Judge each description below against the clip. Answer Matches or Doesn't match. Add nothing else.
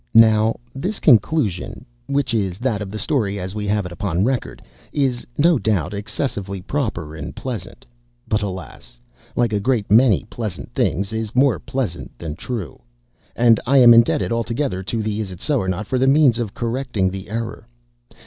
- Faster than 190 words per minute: Doesn't match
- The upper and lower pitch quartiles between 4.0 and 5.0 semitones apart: Matches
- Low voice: Matches